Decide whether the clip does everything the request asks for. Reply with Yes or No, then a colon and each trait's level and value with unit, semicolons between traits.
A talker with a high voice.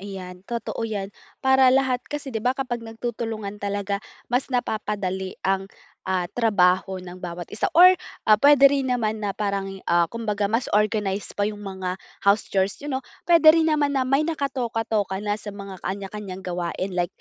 Yes: high, 210 Hz